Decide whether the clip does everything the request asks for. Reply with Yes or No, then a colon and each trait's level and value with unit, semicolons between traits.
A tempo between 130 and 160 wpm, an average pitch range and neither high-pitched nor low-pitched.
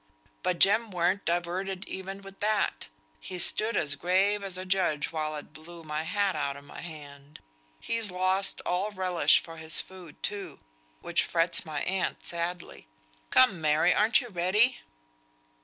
Yes: average, 155 wpm; average, 3.5 semitones; medium, 180 Hz